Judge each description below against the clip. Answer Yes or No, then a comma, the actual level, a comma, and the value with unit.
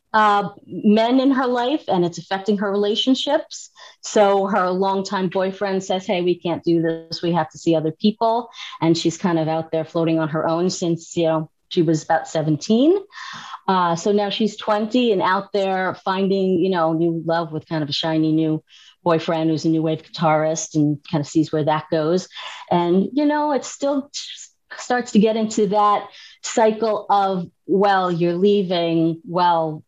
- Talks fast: No, average, 185 wpm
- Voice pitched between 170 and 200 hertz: Yes, medium, 185 Hz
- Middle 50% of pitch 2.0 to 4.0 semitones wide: No, average, 4.6 semitones